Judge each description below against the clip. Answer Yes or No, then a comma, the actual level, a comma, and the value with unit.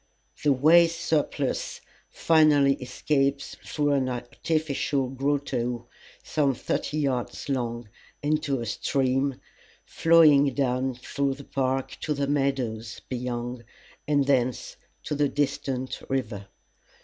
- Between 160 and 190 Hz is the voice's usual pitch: No, low, 135 Hz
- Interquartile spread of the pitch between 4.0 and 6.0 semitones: No, narrow, 2.5 semitones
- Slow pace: Yes, slow, 110 wpm